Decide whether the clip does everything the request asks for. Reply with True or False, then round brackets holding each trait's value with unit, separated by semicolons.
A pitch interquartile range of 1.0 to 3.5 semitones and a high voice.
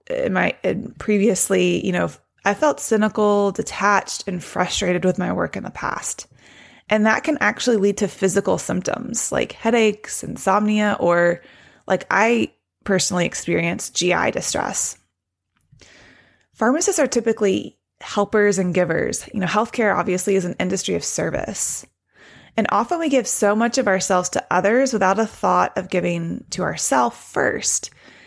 True (3.0 semitones; 205 Hz)